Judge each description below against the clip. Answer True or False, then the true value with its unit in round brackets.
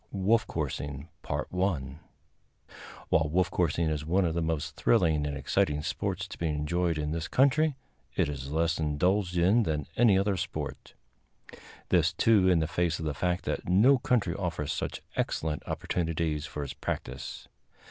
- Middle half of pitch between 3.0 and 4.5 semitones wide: True (3.9 semitones)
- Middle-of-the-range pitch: False (85 Hz)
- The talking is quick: False (160 wpm)